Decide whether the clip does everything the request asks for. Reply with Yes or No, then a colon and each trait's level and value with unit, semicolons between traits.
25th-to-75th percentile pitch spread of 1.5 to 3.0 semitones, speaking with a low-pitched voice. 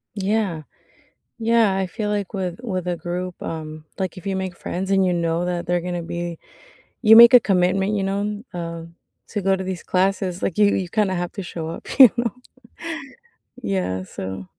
No: narrow, 2.6 semitones; medium, 185 Hz